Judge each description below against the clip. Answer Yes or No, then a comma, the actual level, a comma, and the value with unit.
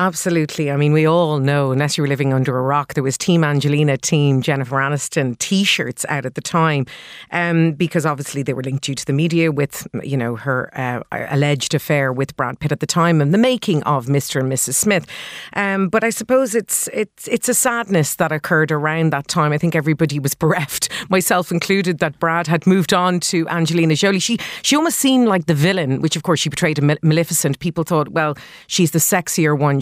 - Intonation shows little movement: No, average, 3.8 semitones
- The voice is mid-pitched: Yes, medium, 160 Hz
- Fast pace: Yes, fast, 215 wpm